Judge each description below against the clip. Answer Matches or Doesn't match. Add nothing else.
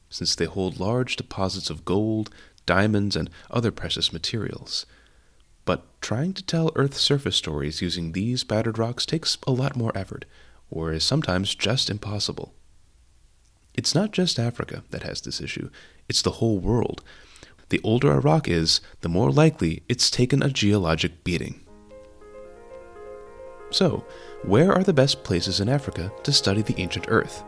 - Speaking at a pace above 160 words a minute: Doesn't match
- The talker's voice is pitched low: Matches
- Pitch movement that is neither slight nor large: Doesn't match